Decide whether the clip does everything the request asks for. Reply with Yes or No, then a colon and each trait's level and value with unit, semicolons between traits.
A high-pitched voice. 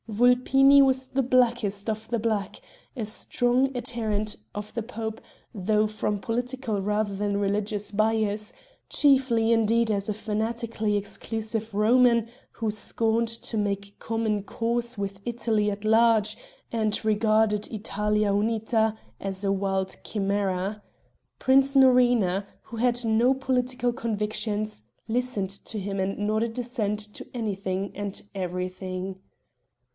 Yes: high, 215 Hz